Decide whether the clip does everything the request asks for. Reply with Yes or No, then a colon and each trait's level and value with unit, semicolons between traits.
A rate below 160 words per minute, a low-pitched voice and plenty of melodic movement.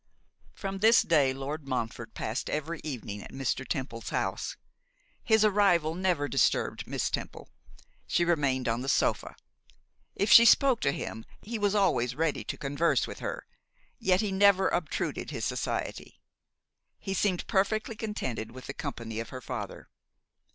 No: average, 150 wpm; medium, 160 Hz; wide, 7.5 semitones